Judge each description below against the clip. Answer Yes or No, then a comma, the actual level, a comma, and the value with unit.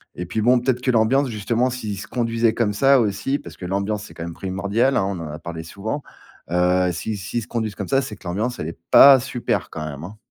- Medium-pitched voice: No, low, 105 Hz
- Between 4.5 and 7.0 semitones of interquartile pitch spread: Yes, average, 4.9 semitones